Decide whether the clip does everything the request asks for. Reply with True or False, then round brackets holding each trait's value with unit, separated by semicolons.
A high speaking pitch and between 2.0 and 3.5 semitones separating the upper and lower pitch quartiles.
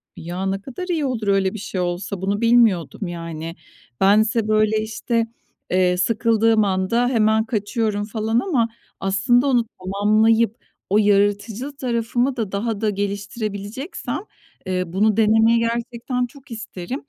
True (215 Hz; 2.9 semitones)